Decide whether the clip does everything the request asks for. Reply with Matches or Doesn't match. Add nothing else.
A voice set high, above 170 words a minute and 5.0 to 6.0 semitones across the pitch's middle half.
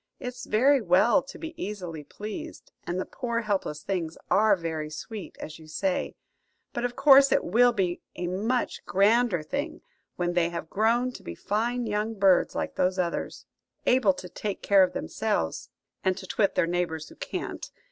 Matches